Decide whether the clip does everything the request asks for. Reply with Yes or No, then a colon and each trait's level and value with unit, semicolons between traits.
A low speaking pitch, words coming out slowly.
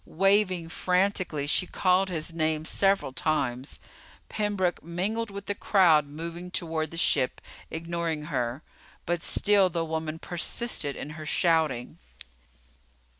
No: medium, 170 Hz; slow, 125 wpm